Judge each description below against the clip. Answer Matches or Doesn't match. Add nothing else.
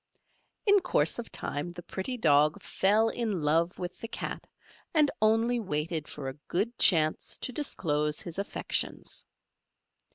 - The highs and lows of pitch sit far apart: Matches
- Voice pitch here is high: Doesn't match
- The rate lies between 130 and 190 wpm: Matches